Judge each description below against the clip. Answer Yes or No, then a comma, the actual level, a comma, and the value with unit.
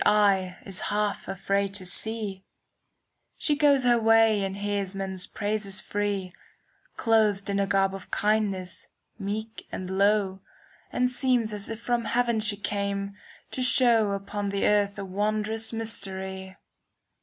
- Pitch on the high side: Yes, high, 205 Hz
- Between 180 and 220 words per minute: No, average, 145 wpm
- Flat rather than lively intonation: Yes, narrow, 2.2 semitones